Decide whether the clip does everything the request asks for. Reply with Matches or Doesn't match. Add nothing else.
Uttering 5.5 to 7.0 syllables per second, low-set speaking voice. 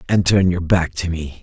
Doesn't match